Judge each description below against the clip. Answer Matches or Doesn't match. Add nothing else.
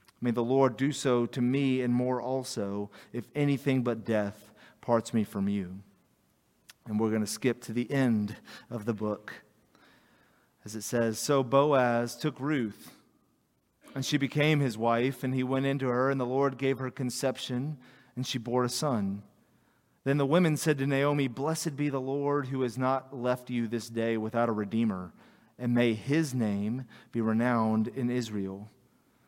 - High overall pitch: Doesn't match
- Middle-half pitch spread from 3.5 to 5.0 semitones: Doesn't match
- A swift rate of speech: Doesn't match